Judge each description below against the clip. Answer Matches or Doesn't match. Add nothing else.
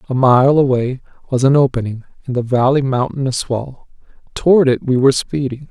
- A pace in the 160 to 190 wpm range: Matches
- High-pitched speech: Doesn't match